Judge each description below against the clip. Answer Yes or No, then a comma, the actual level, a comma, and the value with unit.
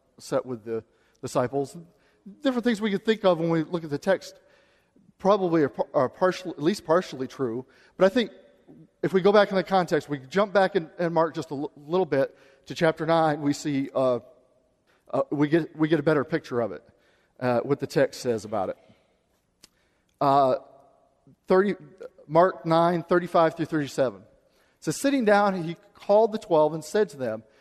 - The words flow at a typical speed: Yes, average, 190 wpm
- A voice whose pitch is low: No, medium, 165 Hz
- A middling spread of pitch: Yes, average, 4.9 semitones